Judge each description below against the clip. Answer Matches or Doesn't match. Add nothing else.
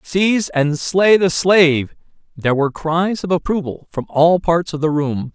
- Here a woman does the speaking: Doesn't match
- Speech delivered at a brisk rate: Doesn't match